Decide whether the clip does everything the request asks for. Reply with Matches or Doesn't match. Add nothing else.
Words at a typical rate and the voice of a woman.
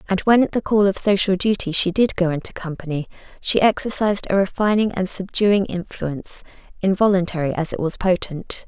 Matches